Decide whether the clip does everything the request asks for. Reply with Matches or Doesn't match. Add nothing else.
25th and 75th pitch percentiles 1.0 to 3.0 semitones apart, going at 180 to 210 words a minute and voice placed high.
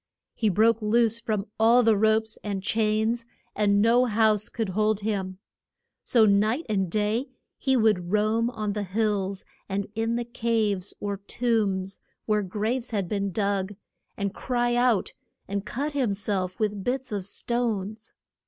Doesn't match